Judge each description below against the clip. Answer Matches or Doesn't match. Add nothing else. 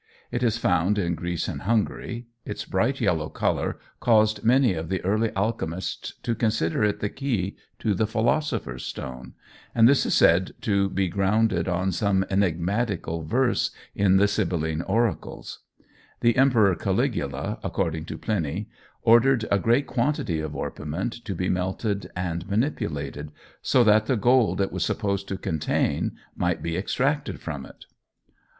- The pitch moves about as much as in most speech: Matches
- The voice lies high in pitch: Doesn't match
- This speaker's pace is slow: Doesn't match